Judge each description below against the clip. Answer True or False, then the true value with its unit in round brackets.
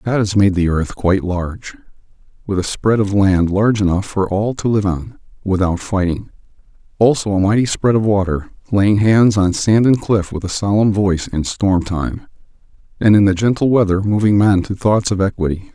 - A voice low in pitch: True (100 Hz)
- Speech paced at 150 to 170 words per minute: False (195 wpm)